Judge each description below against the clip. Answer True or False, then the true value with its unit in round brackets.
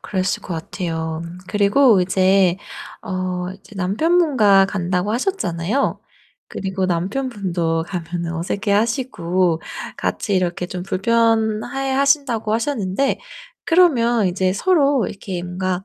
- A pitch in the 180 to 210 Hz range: True (195 Hz)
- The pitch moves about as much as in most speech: True (4.5 semitones)